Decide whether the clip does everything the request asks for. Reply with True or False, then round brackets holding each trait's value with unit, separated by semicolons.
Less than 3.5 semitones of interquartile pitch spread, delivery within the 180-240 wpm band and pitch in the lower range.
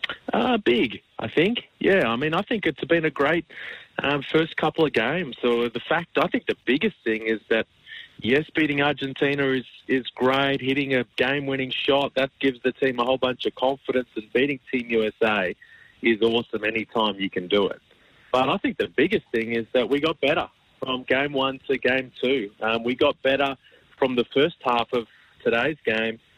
True (3.0 semitones; 200 wpm; 130 Hz)